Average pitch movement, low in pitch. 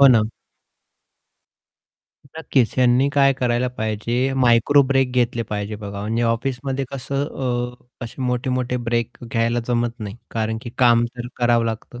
No: narrow, 1.9 semitones; low, 120 Hz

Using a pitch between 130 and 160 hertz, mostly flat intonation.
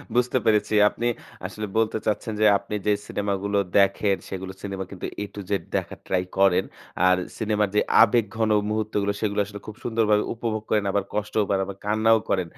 No: low, 105 Hz; narrow, 1.6 semitones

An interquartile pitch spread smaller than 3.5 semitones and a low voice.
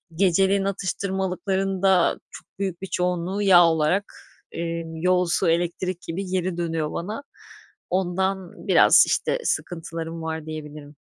No: narrow, 2.5 semitones; medium, 180 Hz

